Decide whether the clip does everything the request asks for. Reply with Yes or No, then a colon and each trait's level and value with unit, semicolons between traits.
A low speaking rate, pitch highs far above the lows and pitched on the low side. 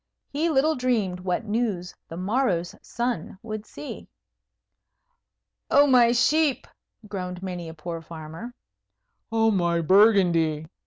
No: slow, 115 wpm; wide, 5.8 semitones; high, 200 Hz